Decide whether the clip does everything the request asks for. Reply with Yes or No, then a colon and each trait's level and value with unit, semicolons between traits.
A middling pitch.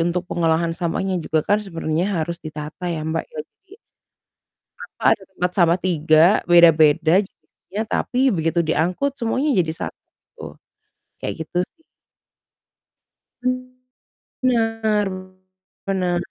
Yes: medium, 175 Hz